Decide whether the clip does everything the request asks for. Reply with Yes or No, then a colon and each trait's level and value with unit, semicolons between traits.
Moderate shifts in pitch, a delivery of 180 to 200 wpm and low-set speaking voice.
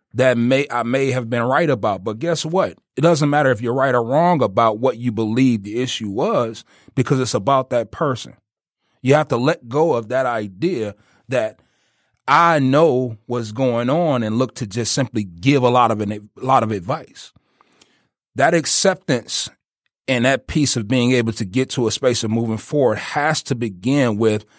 Yes: average, 3.2 semitones; average, 195 wpm; low, 125 Hz